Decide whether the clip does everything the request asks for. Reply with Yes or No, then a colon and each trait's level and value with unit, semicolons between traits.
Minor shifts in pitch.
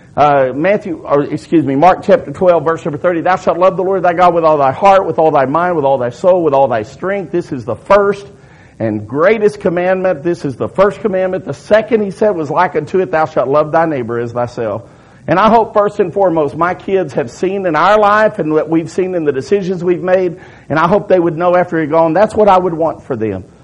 No: average, 3.9 semitones